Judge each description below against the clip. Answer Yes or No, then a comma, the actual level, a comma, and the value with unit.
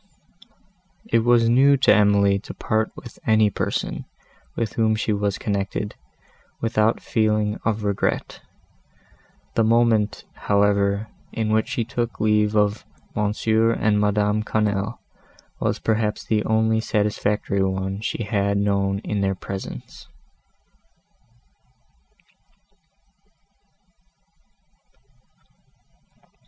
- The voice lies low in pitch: Yes, low, 105 Hz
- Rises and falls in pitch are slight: Yes, narrow, 1.6 semitones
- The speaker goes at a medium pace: No, slow, 100 wpm